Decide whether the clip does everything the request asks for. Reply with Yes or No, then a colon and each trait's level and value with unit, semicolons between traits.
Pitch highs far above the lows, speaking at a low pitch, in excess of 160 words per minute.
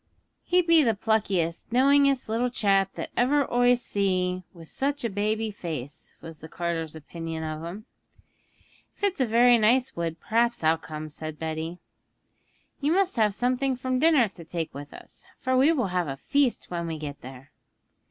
No: wide, 7.6 semitones; high, 205 Hz; average, 175 wpm